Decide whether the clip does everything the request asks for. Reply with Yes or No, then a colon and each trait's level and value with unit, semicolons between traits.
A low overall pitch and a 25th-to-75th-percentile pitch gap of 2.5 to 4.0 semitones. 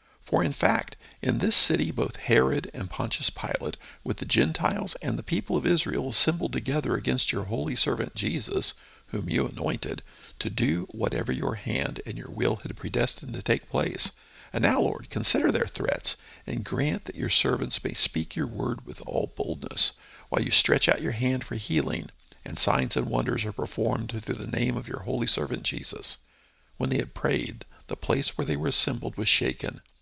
No: low, 115 Hz; average, 4.5 semitones